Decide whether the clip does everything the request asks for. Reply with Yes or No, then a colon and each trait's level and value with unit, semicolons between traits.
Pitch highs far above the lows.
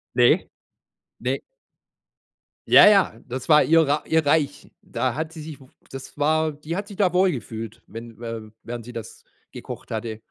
Yes: wide, 5.7 semitones